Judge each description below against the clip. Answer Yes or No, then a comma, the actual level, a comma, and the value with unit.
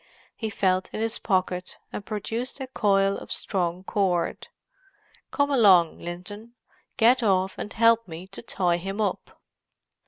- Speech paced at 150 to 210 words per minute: No, slow, 135 wpm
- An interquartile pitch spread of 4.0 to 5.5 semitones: No, average, 3.5 semitones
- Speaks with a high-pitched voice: Yes, high, 200 Hz